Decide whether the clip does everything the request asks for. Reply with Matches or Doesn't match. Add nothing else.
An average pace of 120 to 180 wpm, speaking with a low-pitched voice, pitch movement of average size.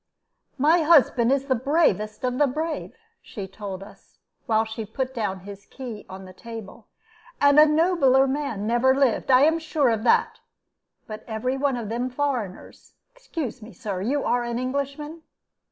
Doesn't match